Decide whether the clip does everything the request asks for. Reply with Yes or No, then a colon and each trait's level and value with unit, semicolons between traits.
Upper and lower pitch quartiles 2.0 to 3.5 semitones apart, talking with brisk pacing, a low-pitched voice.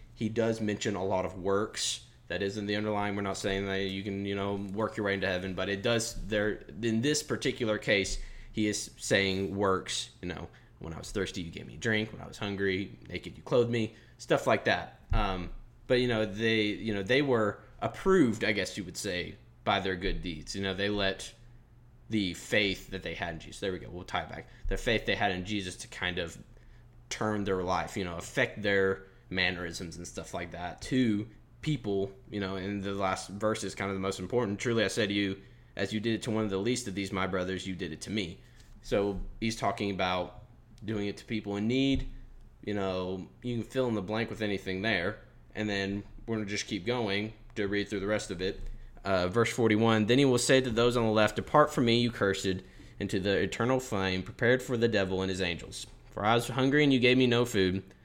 Yes: average, 3.1 semitones; fast, 235 wpm; low, 100 Hz